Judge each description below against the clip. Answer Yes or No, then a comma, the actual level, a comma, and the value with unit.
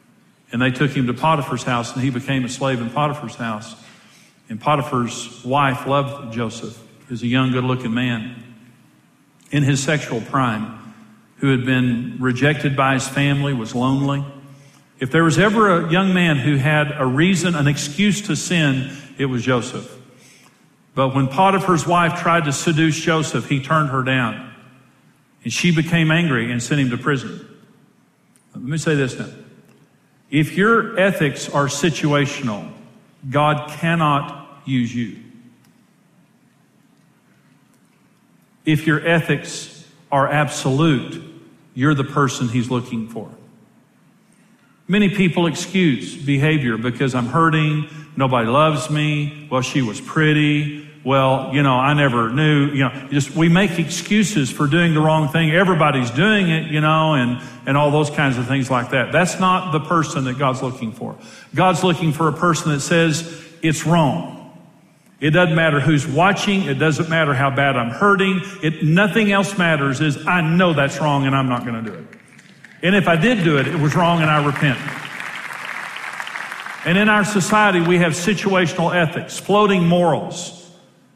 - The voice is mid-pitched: Yes, medium, 150 Hz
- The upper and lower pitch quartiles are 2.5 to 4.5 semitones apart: Yes, average, 4.0 semitones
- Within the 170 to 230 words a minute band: No, average, 160 wpm